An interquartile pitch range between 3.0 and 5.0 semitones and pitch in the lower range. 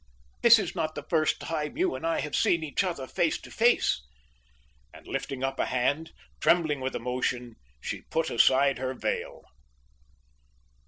No: average, 4.1 semitones; medium, 150 Hz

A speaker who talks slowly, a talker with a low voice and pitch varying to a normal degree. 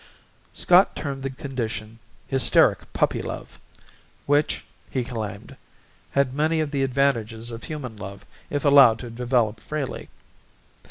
Yes: slow, 125 wpm; low, 130 Hz; average, 3.7 semitones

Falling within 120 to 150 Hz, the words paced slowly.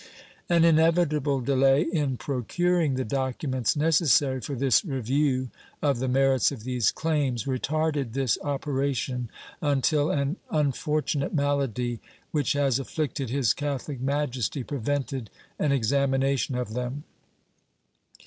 Yes: medium, 140 Hz; slow, 115 wpm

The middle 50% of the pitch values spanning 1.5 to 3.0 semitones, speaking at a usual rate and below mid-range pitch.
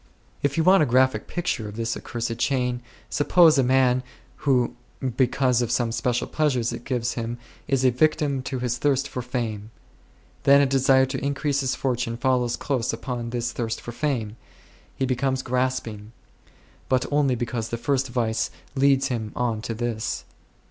Yes: narrow, 2.4 semitones; average, 170 wpm; low, 125 Hz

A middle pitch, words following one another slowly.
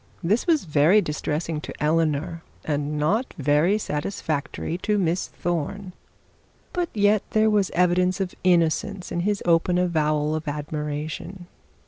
Yes: medium, 170 Hz; slow, 130 wpm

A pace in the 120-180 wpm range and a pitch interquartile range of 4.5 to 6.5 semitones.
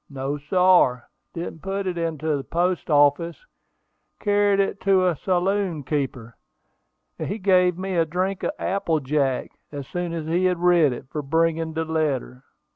No: average, 165 wpm; average, 3.9 semitones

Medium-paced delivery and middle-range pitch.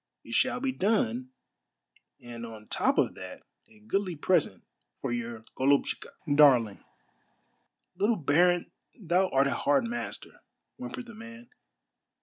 No: slow, 130 wpm; medium, 150 Hz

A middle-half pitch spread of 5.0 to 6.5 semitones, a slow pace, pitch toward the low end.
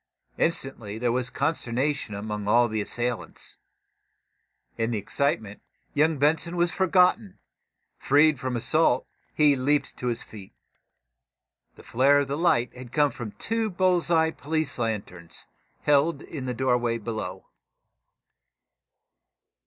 Yes: average, 5.3 semitones; slow, 125 wpm; low, 130 Hz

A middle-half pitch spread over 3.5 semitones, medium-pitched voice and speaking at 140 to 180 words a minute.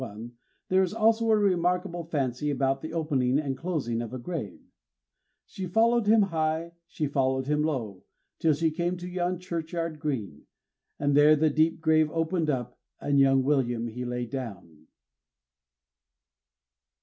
Yes: average, 4.8 semitones; medium, 150 Hz; average, 150 wpm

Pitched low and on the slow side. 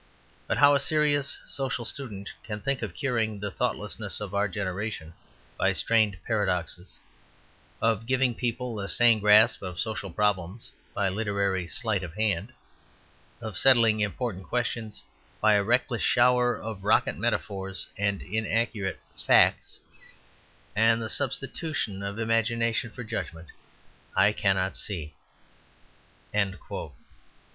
Yes: low, 110 Hz; slow, 120 wpm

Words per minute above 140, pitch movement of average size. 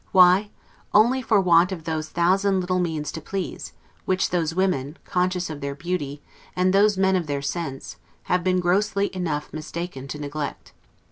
Yes: average, 165 wpm; average, 3.5 semitones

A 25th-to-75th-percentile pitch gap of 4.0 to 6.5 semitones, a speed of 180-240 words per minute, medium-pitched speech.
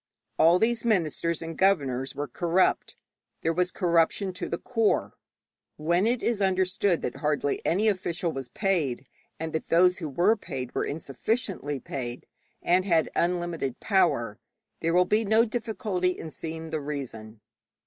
No: average, 4.4 semitones; average, 150 wpm; medium, 170 Hz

